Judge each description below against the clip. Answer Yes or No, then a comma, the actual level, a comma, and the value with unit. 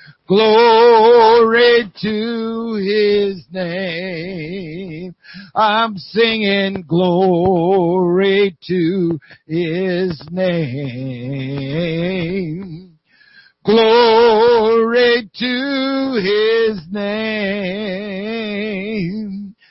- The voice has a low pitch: No, high, 195 Hz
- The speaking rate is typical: No, slow, 45 wpm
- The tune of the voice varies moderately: Yes, average, 4.0 semitones